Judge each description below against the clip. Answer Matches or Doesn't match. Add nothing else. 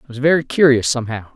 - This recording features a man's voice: Matches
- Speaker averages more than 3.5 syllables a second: Matches